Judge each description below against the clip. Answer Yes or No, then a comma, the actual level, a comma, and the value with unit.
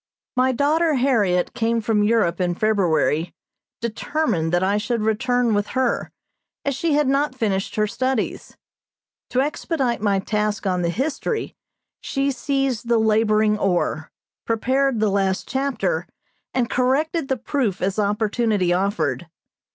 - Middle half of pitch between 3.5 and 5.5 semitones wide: Yes, average, 4.7 semitones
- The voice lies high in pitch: Yes, high, 225 Hz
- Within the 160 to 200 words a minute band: No, slow, 135 wpm